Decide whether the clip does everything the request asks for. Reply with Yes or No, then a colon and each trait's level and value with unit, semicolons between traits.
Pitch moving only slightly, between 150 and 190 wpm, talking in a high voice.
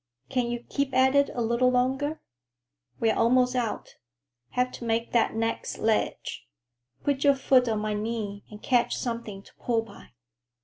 Yes: narrow, 2.3 semitones; average, 165 wpm; high, 240 Hz